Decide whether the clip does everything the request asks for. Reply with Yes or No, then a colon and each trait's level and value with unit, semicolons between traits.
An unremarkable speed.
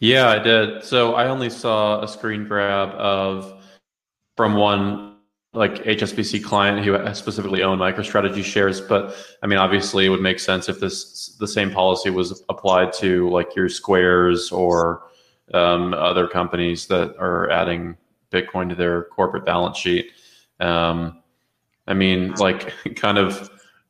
Yes: average, 150 wpm